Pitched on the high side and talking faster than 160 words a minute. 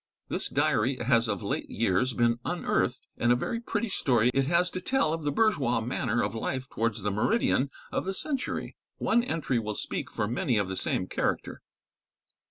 No: low, 125 Hz; average, 185 wpm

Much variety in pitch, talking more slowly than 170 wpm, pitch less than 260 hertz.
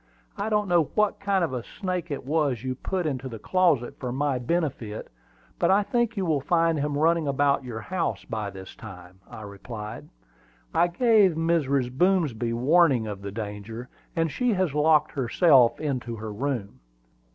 No: wide, 6.8 semitones; average, 175 wpm; medium, 140 Hz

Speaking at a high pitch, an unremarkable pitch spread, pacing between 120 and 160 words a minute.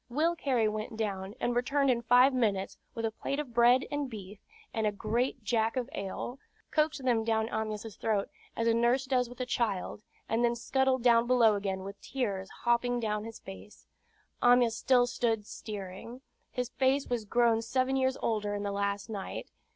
No: high, 230 Hz; average, 3.0 semitones; average, 180 wpm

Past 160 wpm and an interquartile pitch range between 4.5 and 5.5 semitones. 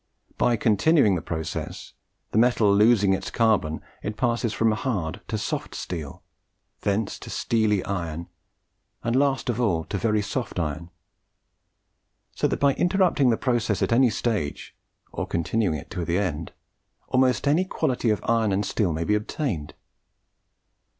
No: average, 150 wpm; average, 4.9 semitones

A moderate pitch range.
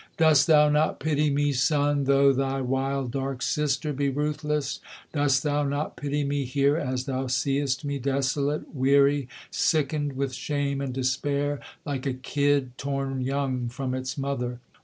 No: narrow, 1.5 semitones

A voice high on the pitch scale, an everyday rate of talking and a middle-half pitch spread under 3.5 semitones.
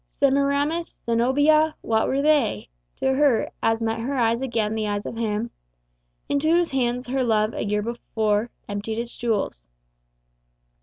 No: high, 235 Hz; average, 150 wpm; average, 4.0 semitones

